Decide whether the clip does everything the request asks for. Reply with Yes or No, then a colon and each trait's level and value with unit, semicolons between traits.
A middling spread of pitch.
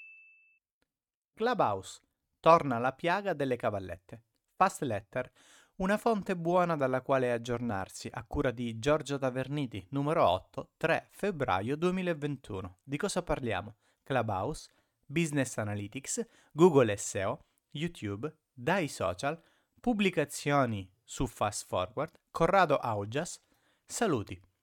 No: wide, 6.3 semitones